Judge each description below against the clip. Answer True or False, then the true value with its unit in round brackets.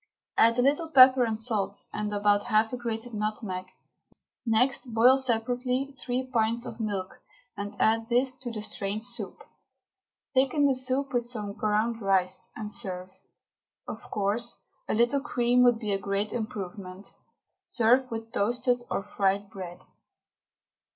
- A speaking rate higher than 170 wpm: False (145 wpm)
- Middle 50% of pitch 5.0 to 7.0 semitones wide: False (3.3 semitones)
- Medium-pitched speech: False (225 Hz)